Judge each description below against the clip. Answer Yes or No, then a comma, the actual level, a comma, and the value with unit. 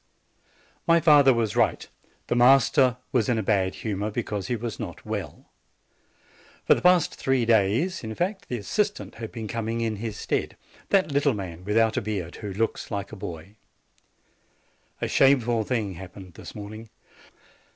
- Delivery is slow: No, average, 165 wpm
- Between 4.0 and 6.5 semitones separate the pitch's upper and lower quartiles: Yes, average, 4.3 semitones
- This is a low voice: Yes, low, 115 Hz